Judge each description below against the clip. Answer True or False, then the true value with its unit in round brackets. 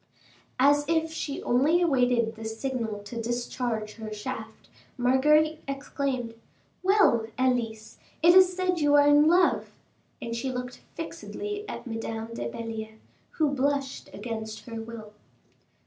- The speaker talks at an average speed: False (130 wpm)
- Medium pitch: False (250 Hz)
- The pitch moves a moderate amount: True (4.6 semitones)